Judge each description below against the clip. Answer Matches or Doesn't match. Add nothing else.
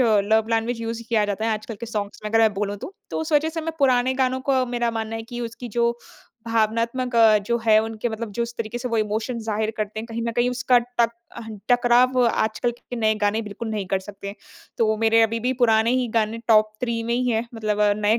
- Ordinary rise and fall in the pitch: Doesn't match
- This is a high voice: Matches